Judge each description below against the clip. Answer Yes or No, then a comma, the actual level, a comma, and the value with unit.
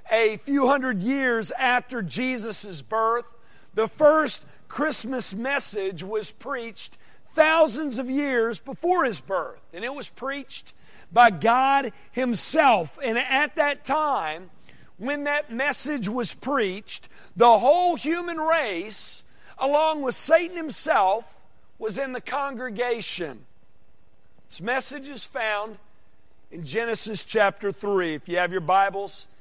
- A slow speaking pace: Yes, slow, 120 wpm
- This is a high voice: Yes, high, 240 Hz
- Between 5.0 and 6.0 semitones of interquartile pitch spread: Yes, wide, 5.6 semitones